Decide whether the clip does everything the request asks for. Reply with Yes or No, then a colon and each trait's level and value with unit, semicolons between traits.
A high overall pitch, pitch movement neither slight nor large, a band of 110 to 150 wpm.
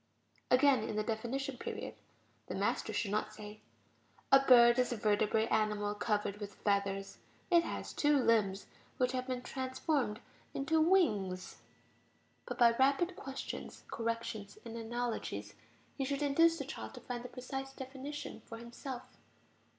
Yes: high, 240 Hz; average, 4.2 semitones; average, 145 wpm